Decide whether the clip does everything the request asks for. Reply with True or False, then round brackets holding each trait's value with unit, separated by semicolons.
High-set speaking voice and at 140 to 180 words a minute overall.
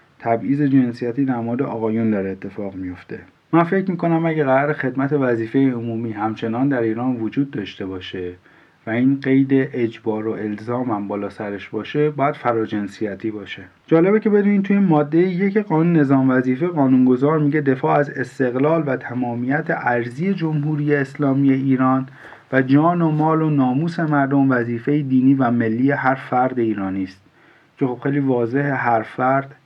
False (130 Hz; 155 wpm)